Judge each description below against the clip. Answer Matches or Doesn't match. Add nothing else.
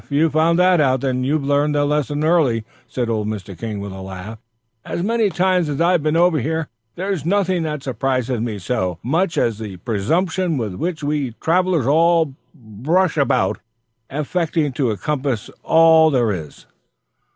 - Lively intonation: Matches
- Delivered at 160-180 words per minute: Matches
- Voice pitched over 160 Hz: Doesn't match